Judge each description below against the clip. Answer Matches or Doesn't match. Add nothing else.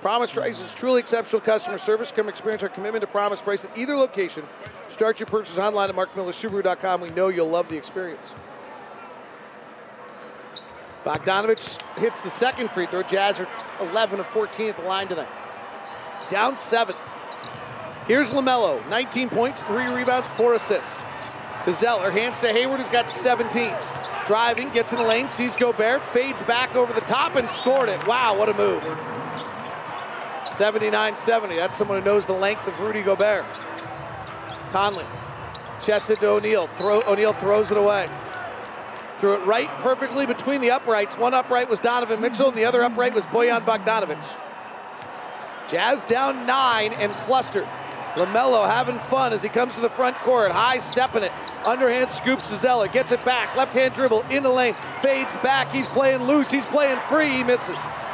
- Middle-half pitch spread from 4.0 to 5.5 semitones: Doesn't match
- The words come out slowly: Doesn't match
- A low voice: Doesn't match